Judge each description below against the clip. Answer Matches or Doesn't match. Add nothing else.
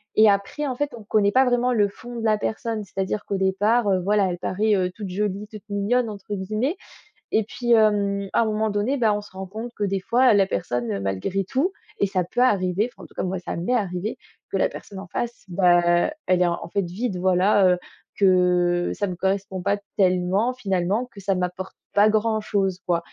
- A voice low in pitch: Doesn't match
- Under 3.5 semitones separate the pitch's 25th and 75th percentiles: Matches